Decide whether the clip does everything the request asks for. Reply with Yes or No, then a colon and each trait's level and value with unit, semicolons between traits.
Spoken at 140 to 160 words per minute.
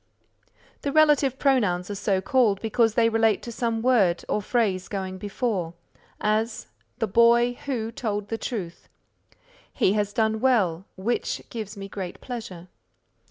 Yes: average, 145 wpm